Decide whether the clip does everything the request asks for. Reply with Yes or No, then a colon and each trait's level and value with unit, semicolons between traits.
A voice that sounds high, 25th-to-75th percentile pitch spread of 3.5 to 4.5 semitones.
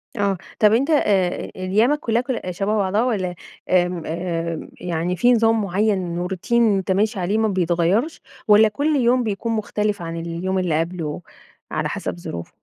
Yes: high, 195 Hz; average, 4.0 semitones